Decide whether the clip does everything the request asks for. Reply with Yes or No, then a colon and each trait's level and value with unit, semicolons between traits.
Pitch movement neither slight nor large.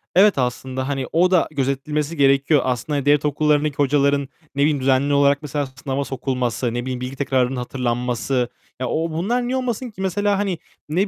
Yes: average, 3.2 semitones